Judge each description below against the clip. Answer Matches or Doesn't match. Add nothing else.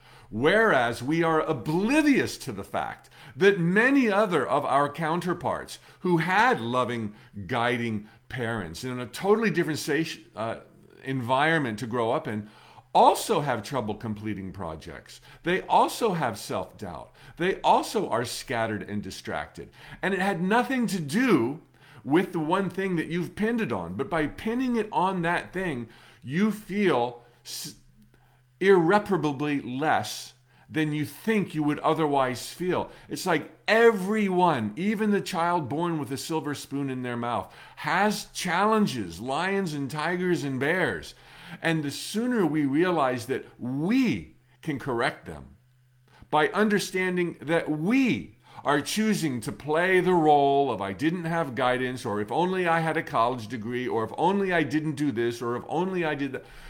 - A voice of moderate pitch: Matches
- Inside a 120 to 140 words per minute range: Doesn't match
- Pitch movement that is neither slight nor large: Doesn't match